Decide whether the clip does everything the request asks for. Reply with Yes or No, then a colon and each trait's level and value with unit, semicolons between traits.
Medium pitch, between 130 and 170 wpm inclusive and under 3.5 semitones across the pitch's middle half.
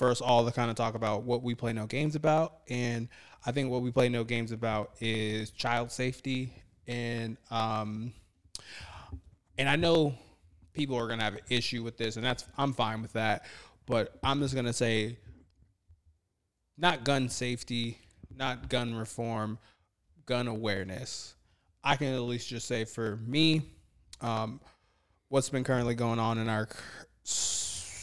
No: low, 115 Hz; average, 160 wpm; average, 3.1 semitones